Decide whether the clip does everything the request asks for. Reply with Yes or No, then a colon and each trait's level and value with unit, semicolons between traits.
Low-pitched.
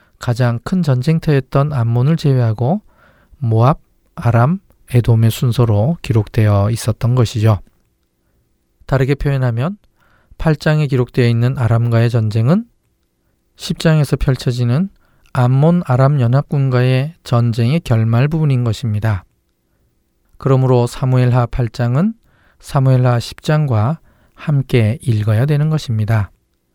Yes: low, 125 Hz